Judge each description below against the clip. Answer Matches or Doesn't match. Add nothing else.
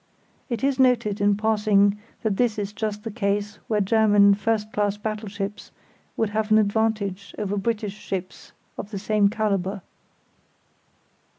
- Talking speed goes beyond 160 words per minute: Doesn't match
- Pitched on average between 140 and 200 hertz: Doesn't match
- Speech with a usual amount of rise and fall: Doesn't match